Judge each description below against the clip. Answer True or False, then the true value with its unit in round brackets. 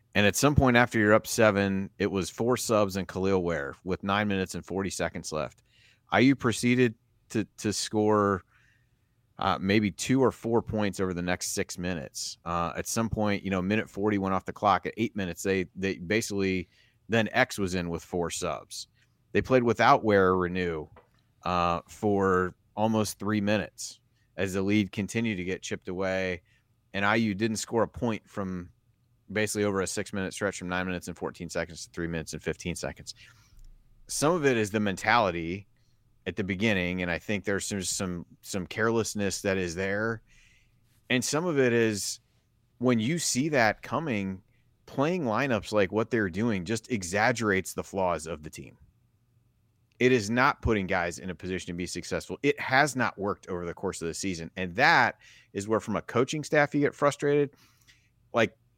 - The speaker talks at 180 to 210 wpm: True (185 wpm)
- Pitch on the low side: True (105 Hz)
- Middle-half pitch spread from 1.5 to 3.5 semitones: False (3.9 semitones)